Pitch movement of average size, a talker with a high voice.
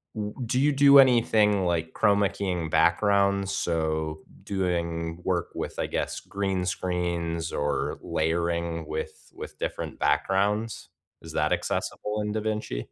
No: average, 3.9 semitones; very low, 95 Hz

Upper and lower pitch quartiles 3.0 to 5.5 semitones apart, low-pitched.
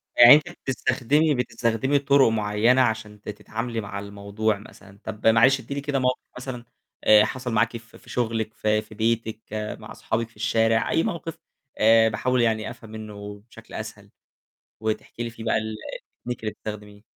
No: narrow, 2.5 semitones; low, 115 Hz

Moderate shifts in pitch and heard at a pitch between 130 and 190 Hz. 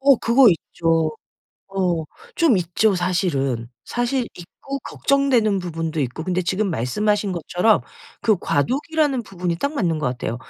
No: wide, 6.3 semitones; medium, 185 Hz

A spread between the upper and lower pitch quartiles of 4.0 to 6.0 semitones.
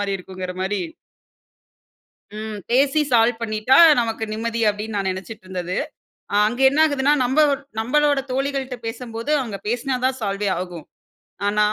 Yes: average, 4.4 semitones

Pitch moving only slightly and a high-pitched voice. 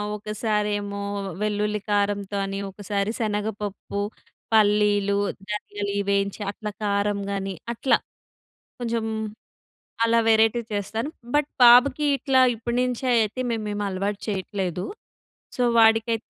Yes: narrow, 1.9 semitones; high, 210 Hz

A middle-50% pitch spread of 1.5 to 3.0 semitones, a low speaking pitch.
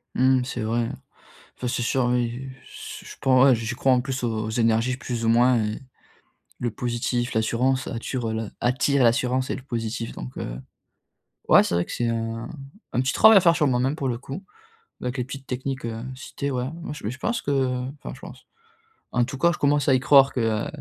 Yes: narrow, 2.4 semitones; low, 125 Hz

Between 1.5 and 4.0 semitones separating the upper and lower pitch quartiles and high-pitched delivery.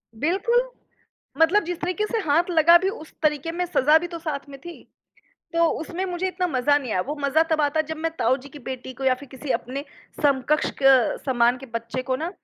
No: average, 4.5 semitones; very high, 305 Hz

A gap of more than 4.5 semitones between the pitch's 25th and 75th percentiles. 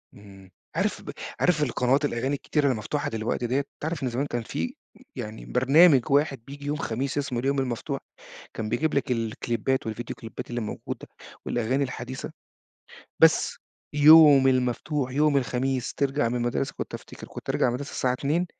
No: average, 3.1 semitones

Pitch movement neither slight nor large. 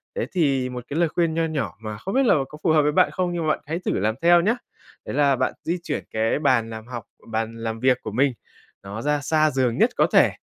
No: wide, 6.2 semitones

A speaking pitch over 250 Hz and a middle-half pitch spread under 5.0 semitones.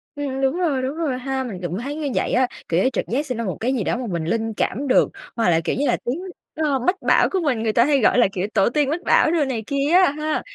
Yes: very high, 265 Hz; average, 4.4 semitones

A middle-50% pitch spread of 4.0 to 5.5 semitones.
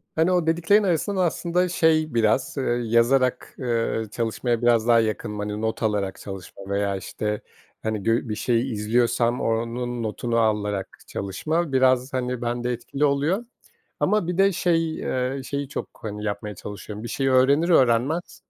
Yes: average, 5.1 semitones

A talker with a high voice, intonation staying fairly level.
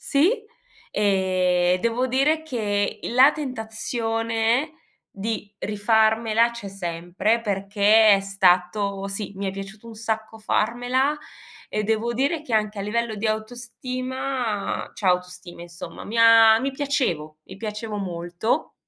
No: high, 220 Hz; average, 3.2 semitones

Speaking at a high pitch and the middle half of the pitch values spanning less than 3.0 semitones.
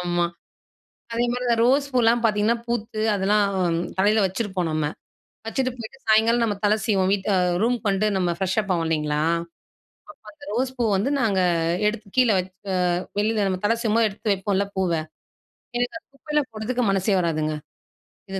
No: high, 210 Hz; average, 3.5 semitones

